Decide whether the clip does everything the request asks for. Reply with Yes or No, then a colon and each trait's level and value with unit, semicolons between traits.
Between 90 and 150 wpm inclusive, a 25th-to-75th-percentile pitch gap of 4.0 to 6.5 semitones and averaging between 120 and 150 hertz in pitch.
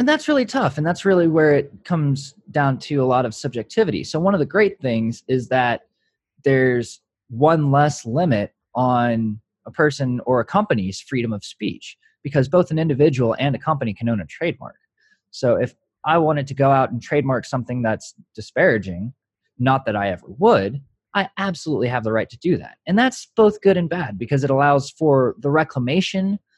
No: average, 190 wpm; average, 5.1 semitones; medium, 140 Hz